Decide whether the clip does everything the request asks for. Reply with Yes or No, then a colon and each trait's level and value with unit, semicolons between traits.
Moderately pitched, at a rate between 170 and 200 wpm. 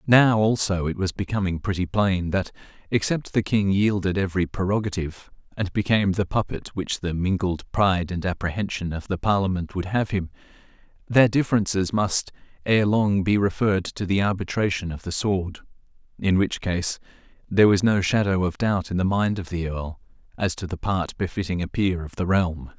No: very low, 95 Hz; average, 180 wpm